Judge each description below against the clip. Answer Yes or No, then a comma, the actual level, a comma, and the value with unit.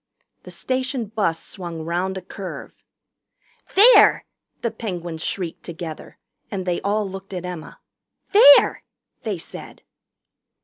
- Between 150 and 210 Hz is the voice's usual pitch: Yes, high, 190 Hz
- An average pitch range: Yes, average, 4.0 semitones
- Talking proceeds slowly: Yes, slow, 120 wpm